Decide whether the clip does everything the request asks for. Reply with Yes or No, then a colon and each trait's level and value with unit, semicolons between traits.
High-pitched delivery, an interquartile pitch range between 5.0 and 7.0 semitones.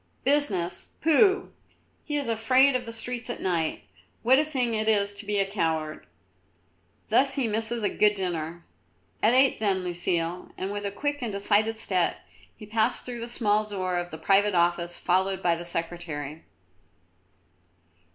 Yes: high, 205 Hz; average, 5.3 semitones